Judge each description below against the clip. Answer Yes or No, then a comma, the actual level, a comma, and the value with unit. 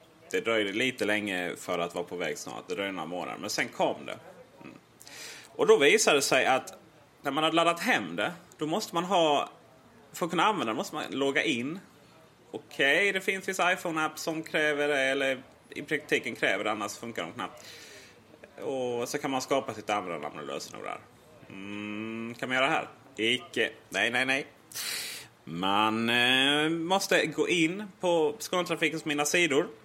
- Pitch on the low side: No, medium, 145 Hz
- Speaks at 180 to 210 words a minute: Yes, average, 185 wpm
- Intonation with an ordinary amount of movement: No, wide, 6.9 semitones